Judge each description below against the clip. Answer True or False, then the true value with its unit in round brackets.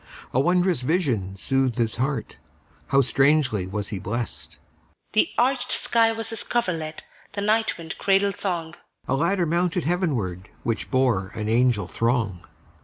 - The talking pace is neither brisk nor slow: False (120 wpm)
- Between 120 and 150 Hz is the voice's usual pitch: True (140 Hz)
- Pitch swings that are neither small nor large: False (8.0 semitones)